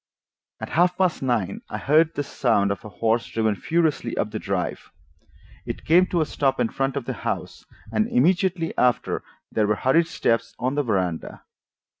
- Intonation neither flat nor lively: No, wide, 6.7 semitones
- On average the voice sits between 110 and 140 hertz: Yes, low, 135 Hz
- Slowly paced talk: No, average, 180 wpm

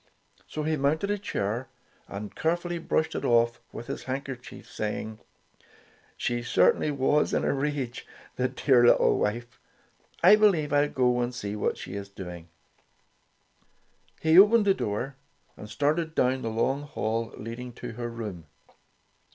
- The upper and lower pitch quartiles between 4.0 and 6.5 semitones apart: Yes, average, 4.7 semitones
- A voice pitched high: No, low, 125 Hz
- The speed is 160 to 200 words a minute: No, average, 150 wpm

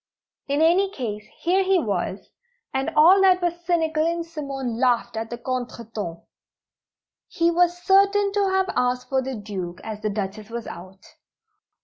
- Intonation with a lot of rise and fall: Yes, wide, 8.0 semitones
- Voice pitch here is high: Yes, very high, 270 Hz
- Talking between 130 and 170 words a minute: Yes, average, 155 wpm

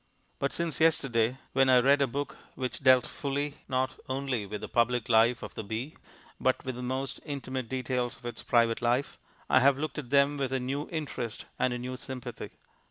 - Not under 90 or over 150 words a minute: No, average, 200 wpm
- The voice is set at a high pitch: No, low, 130 Hz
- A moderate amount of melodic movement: No, narrow, 2.3 semitones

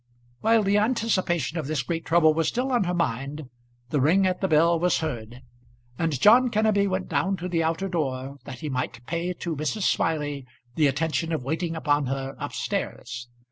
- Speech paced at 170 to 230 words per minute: Yes, average, 190 wpm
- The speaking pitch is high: No, medium, 165 Hz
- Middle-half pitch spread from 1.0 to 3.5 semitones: No, average, 4.8 semitones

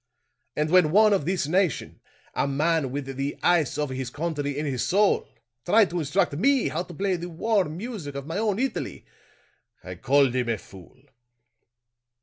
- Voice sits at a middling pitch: Yes, medium, 160 Hz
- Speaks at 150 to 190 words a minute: Yes, average, 175 wpm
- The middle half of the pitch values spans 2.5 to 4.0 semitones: No, wide, 5.4 semitones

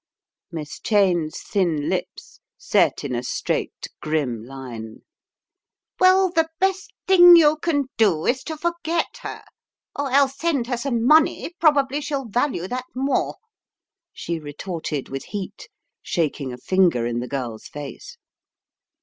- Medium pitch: No, high, 225 Hz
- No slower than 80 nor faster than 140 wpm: Yes, slow, 135 wpm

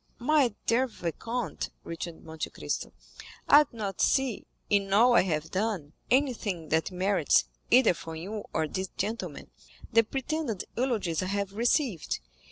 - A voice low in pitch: No, high, 205 Hz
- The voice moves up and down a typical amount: No, wide, 5.8 semitones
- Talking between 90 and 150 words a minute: Yes, average, 145 wpm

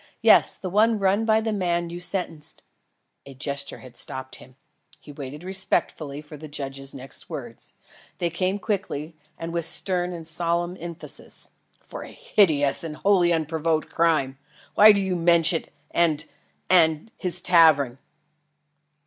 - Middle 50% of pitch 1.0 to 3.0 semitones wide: No, average, 3.6 semitones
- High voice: No, medium, 165 Hz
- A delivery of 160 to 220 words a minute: No, average, 150 wpm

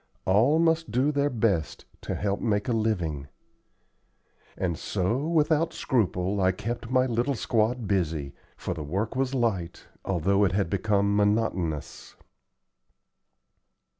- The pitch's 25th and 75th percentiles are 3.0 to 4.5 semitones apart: No, average, 5.1 semitones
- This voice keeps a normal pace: No, slow, 130 wpm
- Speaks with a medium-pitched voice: No, low, 105 Hz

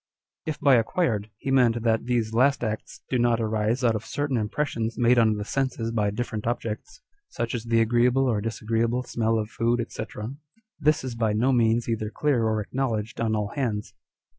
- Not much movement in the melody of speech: Yes, narrow, 2.2 semitones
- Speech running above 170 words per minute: Yes, average, 190 wpm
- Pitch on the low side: Yes, low, 115 Hz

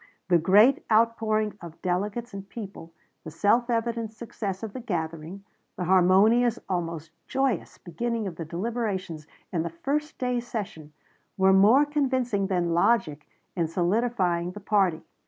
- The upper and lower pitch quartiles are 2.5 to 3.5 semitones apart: No, average, 5.1 semitones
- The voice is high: Yes, high, 200 Hz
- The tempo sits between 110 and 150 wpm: Yes, average, 140 wpm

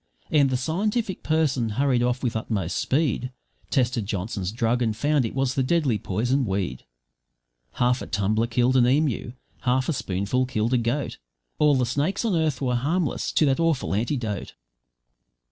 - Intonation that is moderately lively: Yes, average, 4.1 semitones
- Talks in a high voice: No, low, 125 Hz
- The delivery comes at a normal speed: Yes, average, 165 wpm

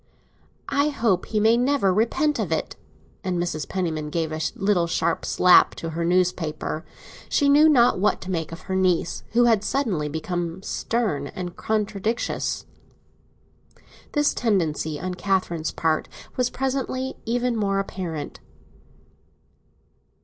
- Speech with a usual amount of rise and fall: No, wide, 6.0 semitones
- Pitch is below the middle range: No, high, 190 Hz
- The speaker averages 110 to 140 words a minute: Yes, slow, 135 wpm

